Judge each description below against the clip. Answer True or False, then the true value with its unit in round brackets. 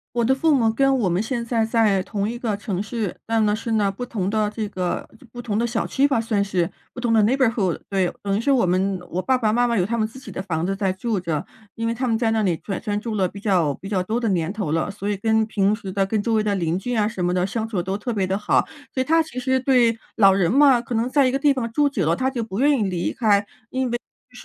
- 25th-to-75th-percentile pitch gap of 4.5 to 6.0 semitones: False (3.6 semitones)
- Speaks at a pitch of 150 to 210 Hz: False (220 Hz)